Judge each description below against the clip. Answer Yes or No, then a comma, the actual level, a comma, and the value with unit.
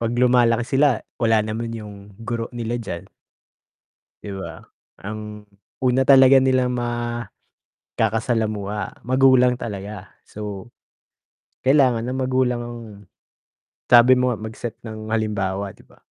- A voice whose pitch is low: Yes, low, 115 Hz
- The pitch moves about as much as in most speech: Yes, average, 3.0 semitones